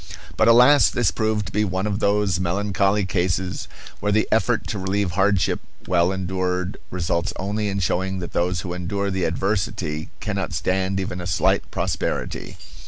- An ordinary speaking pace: Yes, average, 165 wpm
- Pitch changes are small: Yes, narrow, 2.2 semitones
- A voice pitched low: Yes, very low, 95 Hz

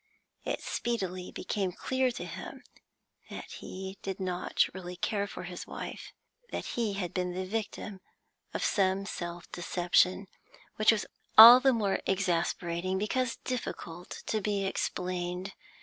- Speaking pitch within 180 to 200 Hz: Yes, high, 190 Hz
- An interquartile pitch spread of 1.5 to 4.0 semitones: Yes, average, 2.8 semitones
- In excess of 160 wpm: No, slow, 135 wpm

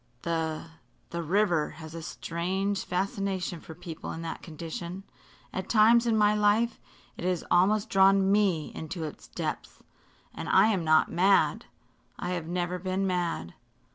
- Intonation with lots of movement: No, average, 3.1 semitones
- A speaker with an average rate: Yes, average, 150 wpm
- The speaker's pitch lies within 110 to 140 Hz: No, medium, 180 Hz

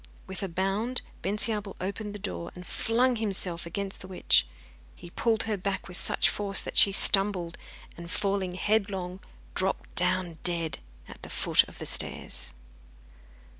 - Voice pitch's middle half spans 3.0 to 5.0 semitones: No, narrow, 2.6 semitones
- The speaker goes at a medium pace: Yes, average, 155 wpm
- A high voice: Yes, high, 195 Hz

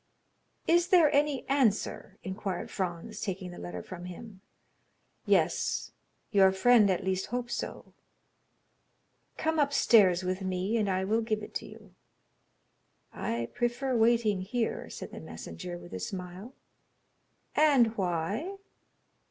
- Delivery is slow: Yes, slow, 125 wpm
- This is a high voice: Yes, high, 205 Hz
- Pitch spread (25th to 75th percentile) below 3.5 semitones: No, average, 4.6 semitones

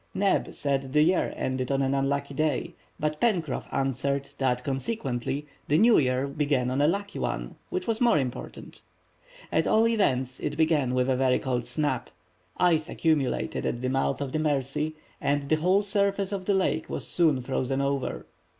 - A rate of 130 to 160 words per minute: No, average, 175 wpm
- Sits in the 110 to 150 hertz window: Yes, medium, 140 Hz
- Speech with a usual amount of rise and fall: Yes, average, 3.9 semitones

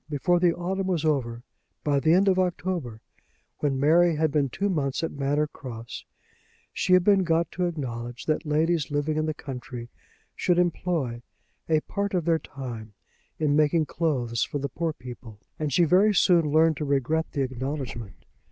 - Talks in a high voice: No, medium, 150 Hz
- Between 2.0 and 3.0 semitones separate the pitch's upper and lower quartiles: No, average, 4.5 semitones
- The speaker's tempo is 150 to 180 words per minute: Yes, average, 175 wpm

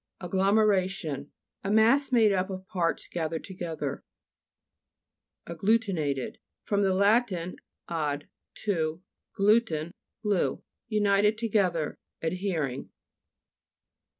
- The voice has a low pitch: No, high, 190 Hz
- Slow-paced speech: Yes, slow, 95 wpm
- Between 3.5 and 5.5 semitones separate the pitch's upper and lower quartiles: Yes, average, 4.4 semitones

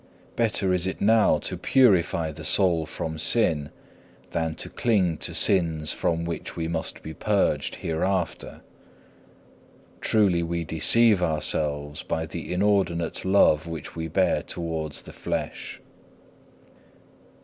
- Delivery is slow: Yes, slow, 125 wpm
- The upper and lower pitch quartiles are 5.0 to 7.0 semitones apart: No, average, 3.0 semitones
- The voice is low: Yes, very low, 85 Hz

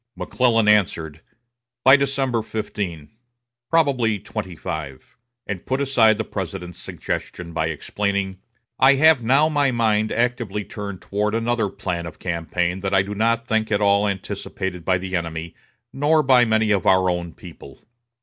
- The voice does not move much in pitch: No, average, 4.6 semitones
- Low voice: Yes, low, 105 Hz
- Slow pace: No, average, 150 wpm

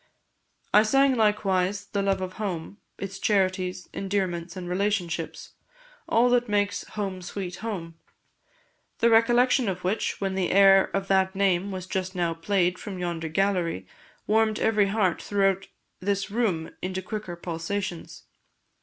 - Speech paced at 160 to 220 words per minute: No, average, 140 wpm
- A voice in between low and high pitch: No, high, 195 Hz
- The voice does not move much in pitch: Yes, narrow, 2.3 semitones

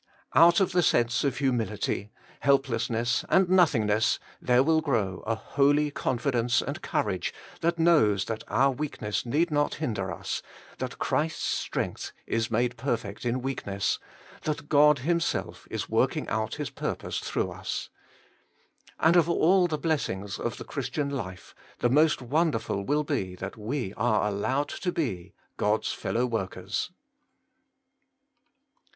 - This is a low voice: Yes, low, 130 Hz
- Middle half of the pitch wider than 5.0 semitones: Yes, wide, 5.6 semitones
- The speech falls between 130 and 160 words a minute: Yes, average, 140 wpm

